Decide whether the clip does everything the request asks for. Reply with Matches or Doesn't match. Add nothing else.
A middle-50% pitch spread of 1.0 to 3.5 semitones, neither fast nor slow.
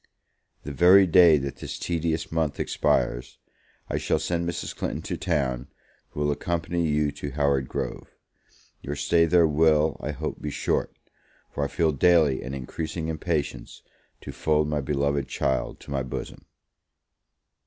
Matches